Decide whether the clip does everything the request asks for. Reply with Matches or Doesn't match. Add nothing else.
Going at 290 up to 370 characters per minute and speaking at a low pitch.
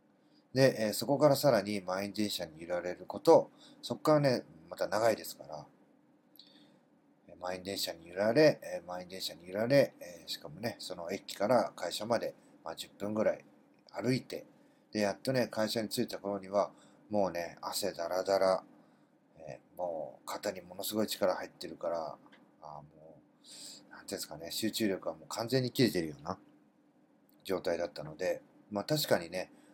Matches